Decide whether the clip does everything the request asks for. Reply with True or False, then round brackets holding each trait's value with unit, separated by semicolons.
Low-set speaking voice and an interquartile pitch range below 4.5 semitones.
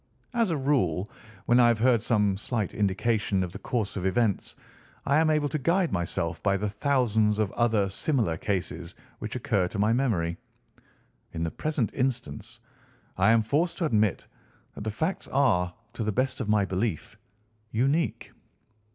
False (110 Hz; 5.0 semitones)